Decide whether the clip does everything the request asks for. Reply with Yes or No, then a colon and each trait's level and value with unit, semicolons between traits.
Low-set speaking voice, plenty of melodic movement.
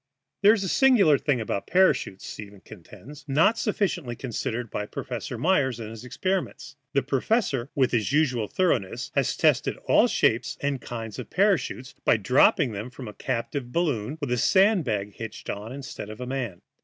Yes: low, 130 Hz; wide, 5.9 semitones